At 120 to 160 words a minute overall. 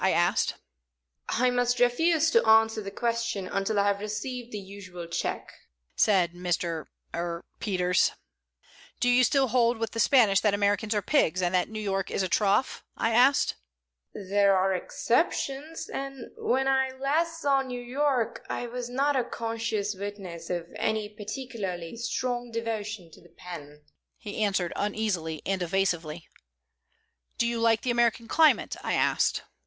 Yes: average, 155 wpm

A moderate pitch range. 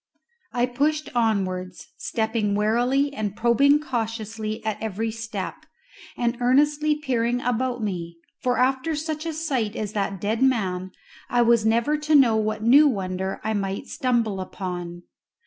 Yes: average, 4.0 semitones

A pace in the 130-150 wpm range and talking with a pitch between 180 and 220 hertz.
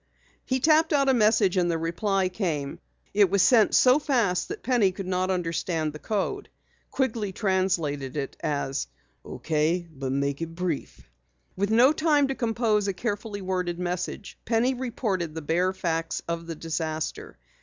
No: average, 160 wpm; medium, 185 Hz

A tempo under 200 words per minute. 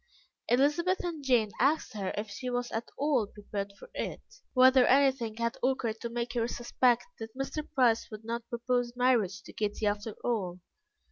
Yes: average, 175 wpm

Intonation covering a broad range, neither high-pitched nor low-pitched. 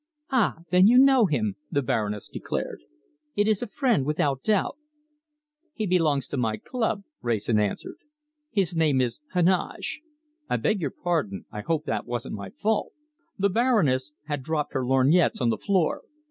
Yes: wide, 8.0 semitones; medium, 155 Hz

